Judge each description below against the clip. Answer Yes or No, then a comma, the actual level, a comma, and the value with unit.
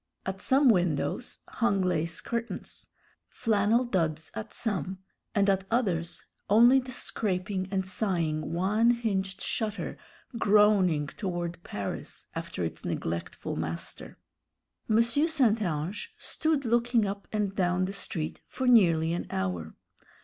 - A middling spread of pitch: Yes, average, 5.0 semitones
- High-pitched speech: Yes, high, 195 Hz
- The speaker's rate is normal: No, slow, 125 wpm